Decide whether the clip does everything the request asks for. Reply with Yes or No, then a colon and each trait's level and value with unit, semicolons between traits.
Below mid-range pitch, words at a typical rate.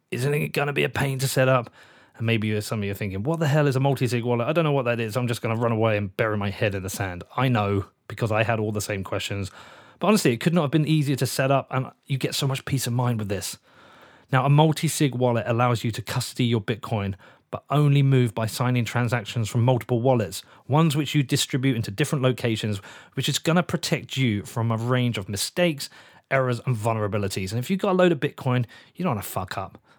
No: low, 125 Hz; fast, 260 wpm